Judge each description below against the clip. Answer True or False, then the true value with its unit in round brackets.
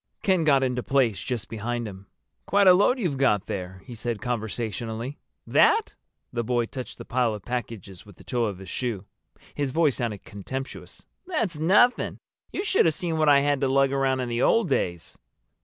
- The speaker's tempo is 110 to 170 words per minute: False (190 wpm)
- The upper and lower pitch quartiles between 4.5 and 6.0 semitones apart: True (4.8 semitones)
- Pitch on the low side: True (125 Hz)